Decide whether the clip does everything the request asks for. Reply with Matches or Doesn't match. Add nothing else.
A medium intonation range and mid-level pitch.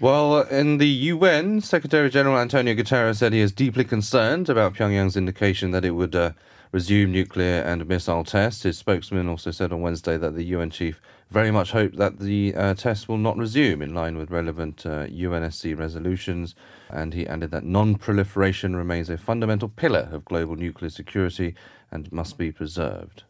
Doesn't match